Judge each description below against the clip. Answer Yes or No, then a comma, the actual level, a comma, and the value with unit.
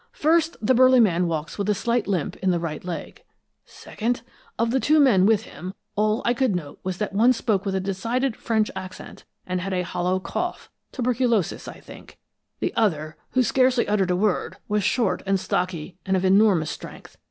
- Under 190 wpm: No, average, 195 wpm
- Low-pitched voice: No, high, 205 Hz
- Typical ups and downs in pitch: Yes, average, 4.6 semitones